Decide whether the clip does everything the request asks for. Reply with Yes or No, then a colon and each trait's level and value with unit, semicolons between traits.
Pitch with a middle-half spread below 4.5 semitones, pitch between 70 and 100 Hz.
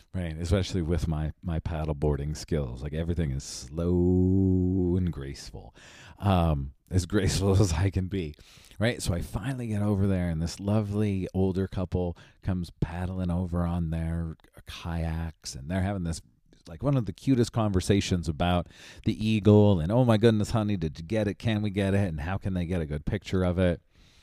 Yes: average, 3.3 semitones; very low, 90 Hz